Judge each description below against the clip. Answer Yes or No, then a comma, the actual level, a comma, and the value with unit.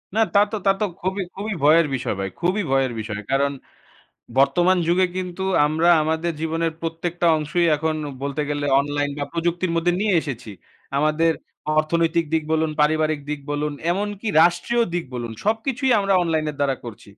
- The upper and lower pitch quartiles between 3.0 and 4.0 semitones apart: Yes, average, 3.5 semitones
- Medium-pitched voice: Yes, medium, 165 Hz